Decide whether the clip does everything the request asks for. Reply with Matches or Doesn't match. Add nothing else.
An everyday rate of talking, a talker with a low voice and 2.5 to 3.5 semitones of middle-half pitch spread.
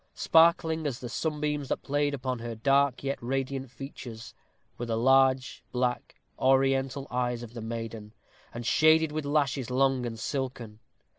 Matches